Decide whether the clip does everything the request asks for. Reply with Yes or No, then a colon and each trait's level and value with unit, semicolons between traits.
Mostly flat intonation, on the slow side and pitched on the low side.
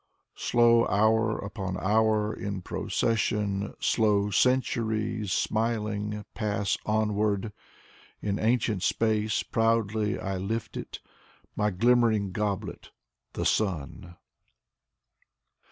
Yes: narrow, 1.7 semitones; slow, 90 wpm; low, 105 Hz